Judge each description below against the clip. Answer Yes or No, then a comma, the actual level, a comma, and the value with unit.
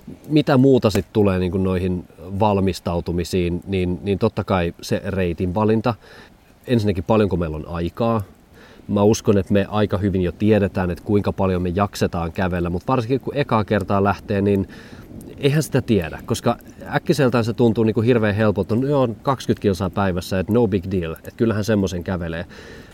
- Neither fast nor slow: No, fast, 170 wpm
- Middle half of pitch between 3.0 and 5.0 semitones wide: Yes, average, 3.5 semitones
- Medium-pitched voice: No, low, 100 Hz